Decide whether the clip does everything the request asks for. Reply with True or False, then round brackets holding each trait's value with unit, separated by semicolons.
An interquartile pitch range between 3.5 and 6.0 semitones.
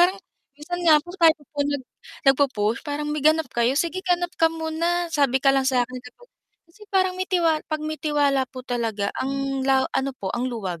True (4.0 semitones)